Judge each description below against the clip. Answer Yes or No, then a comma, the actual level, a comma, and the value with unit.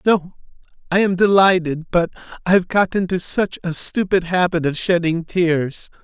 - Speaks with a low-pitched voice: No, medium, 175 Hz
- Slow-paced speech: No, average, 150 wpm